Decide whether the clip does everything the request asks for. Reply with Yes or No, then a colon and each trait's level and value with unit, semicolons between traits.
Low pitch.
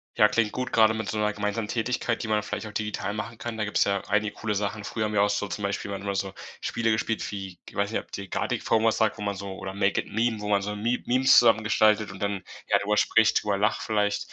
Yes: low, 105 Hz